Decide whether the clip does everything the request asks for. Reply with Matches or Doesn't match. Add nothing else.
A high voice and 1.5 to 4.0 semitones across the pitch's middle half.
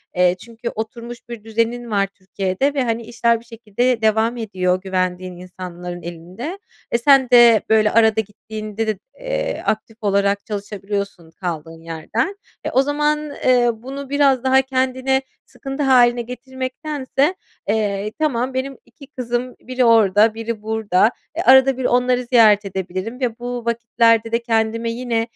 Matches